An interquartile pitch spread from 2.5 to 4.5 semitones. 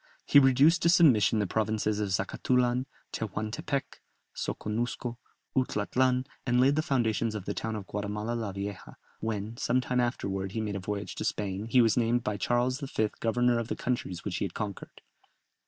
Yes: average, 3.3 semitones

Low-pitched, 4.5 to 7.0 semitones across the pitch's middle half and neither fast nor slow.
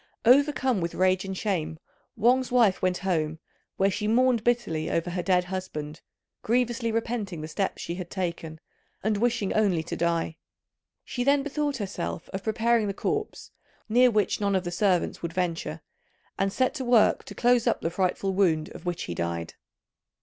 No: high, 195 Hz; wide, 5.5 semitones; average, 175 wpm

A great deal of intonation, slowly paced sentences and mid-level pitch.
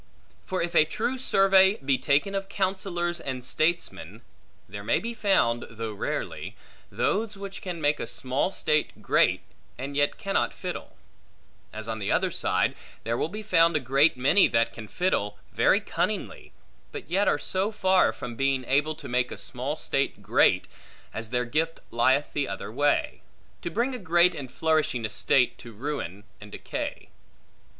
No: wide, 7.2 semitones; average, 170 wpm; medium, 150 Hz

